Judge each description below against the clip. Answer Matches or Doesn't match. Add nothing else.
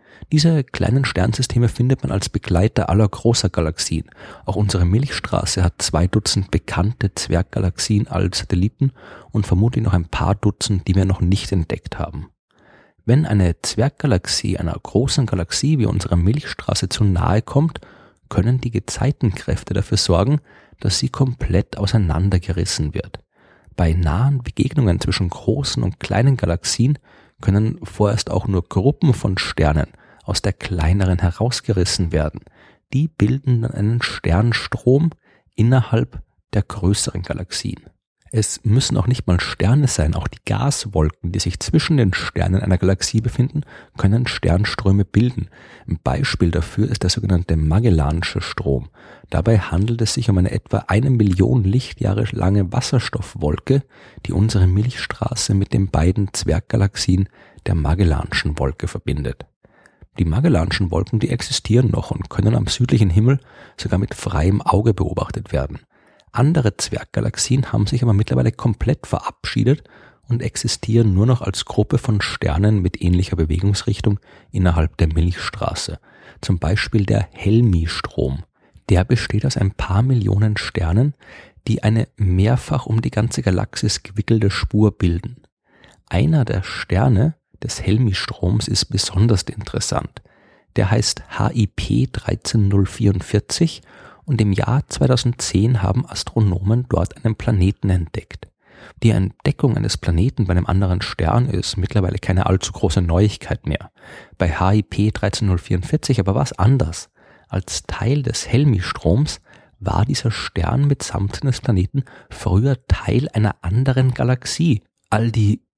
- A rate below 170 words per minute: Matches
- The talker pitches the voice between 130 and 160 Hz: Doesn't match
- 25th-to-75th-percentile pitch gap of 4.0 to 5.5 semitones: Matches